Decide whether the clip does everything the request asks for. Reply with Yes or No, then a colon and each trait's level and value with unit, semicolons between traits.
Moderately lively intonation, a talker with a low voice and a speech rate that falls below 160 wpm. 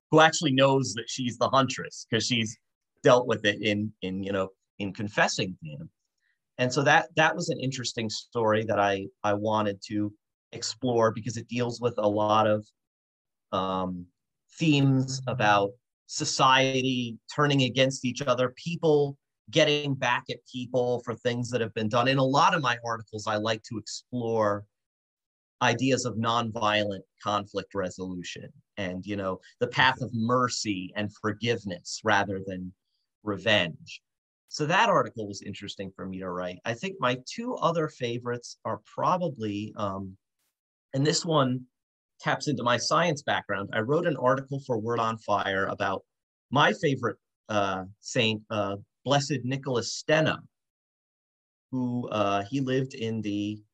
Yes: average, 4.1 semitones; low, 115 Hz; average, 150 wpm